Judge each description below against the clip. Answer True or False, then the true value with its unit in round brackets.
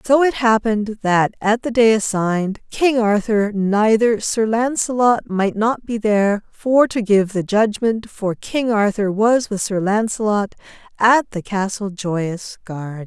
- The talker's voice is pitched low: False (215 Hz)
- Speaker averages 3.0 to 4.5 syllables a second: True (4.0 syllables/s)